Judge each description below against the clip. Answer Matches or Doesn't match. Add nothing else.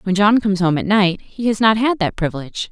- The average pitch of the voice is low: Doesn't match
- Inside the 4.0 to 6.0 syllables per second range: Doesn't match